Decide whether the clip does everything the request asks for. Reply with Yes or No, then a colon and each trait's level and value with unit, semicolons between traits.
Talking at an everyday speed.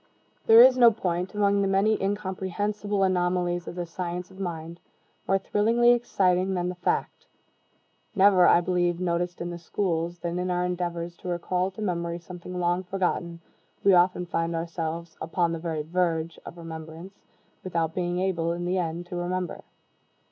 Yes: average, 165 wpm